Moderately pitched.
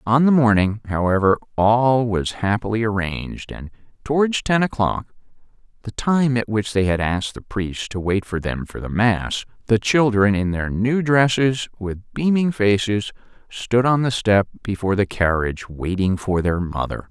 No: low, 110 Hz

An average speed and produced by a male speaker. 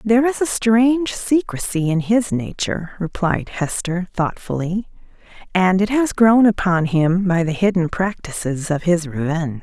No: average, 150 wpm; female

